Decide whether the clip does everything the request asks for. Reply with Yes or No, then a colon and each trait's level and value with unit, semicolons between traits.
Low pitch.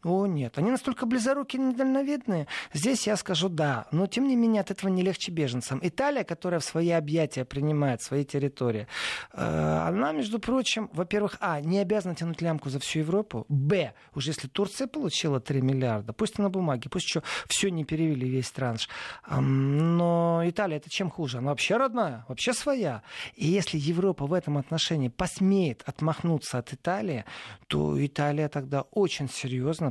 No: medium, 165 Hz